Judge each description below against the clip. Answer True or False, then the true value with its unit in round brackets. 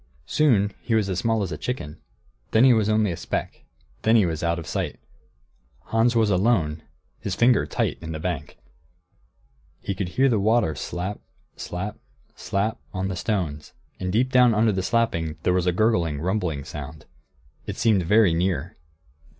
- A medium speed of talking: True (170 wpm)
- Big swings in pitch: False (5.0 semitones)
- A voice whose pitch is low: True (95 Hz)